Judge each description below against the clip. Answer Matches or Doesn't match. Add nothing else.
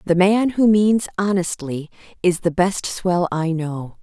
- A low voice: Doesn't match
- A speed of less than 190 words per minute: Matches